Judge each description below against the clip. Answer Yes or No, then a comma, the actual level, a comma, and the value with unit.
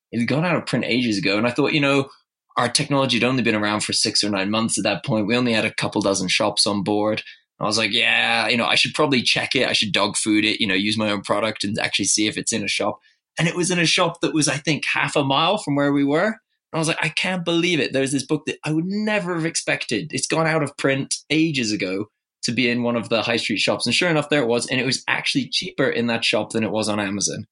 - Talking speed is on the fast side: Yes, fast, 295 wpm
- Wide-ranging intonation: Yes, wide, 6.3 semitones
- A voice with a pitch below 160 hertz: Yes, low, 135 Hz